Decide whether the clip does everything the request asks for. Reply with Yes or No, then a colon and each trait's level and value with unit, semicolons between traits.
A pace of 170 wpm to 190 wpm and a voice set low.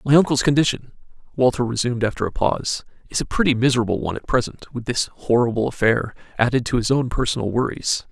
Yes: average, 185 wpm; low, 125 Hz